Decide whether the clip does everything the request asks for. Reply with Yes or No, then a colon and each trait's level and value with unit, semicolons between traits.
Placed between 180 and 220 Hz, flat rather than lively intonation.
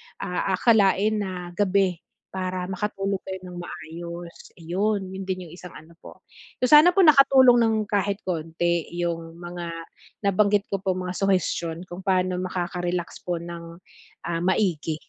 Yes: medium, 185 Hz; narrow, 2.3 semitones